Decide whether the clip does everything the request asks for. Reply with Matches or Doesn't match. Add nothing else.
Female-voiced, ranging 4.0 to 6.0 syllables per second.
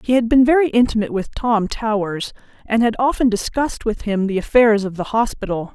Matches